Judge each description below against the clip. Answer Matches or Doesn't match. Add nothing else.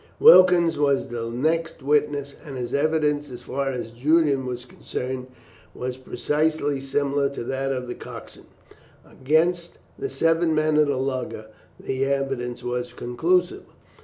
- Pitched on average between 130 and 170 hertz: Matches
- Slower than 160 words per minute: Matches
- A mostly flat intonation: Doesn't match